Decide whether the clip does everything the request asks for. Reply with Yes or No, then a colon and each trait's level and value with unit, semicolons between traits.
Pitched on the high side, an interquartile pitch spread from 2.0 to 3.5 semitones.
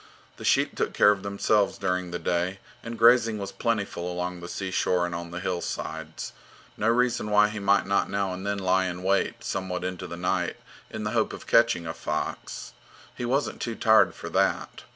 No: very low, 95 Hz; average, 3.0 semitones